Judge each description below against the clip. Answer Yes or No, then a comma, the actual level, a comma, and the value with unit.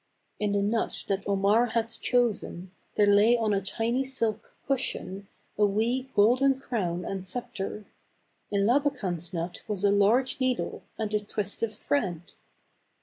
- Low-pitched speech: No, high, 210 Hz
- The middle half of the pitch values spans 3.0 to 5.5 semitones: Yes, average, 3.4 semitones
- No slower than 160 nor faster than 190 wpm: No, average, 145 wpm